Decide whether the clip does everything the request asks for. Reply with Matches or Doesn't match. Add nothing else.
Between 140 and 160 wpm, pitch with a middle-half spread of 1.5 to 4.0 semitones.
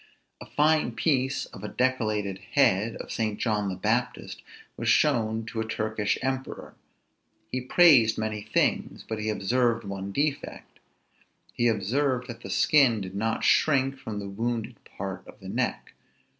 Matches